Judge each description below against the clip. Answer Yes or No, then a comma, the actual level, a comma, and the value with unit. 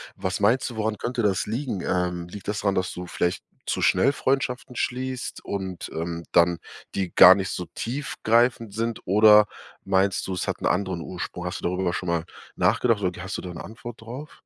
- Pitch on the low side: Yes, low, 100 Hz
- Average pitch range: Yes, average, 4.4 semitones